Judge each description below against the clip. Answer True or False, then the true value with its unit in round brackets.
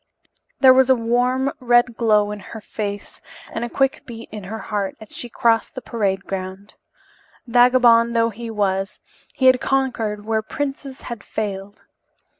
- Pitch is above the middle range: True (230 Hz)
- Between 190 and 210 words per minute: False (160 wpm)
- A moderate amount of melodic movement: True (3.2 semitones)